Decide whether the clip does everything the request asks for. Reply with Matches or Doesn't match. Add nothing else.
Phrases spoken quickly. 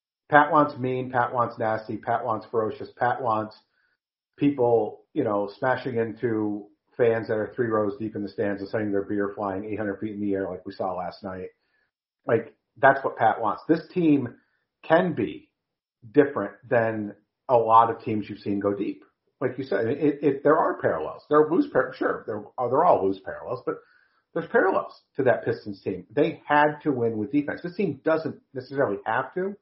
Doesn't match